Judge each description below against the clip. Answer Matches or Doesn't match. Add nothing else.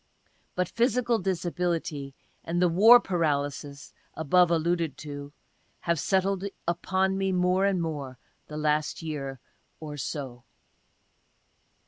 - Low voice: Doesn't match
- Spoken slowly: Matches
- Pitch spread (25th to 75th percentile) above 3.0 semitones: Matches